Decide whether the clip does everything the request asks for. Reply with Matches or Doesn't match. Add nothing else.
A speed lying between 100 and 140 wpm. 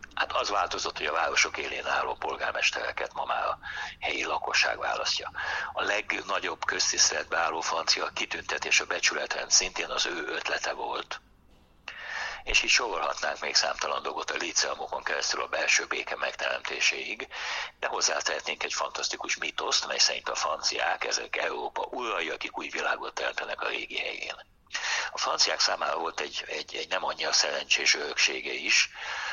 Doesn't match